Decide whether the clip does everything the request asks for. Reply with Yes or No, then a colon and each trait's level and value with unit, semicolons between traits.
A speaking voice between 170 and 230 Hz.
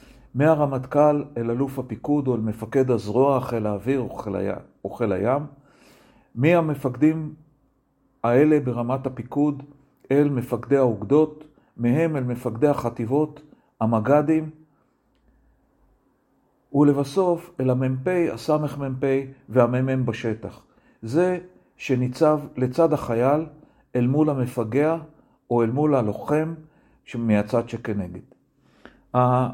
No: low, 135 Hz